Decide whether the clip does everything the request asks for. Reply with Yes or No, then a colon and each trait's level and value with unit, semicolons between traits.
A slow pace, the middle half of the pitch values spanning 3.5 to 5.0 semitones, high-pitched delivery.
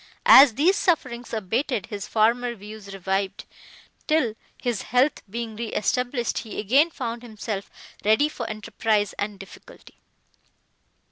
No: slow, 125 wpm; average, 3.1 semitones; high, 230 Hz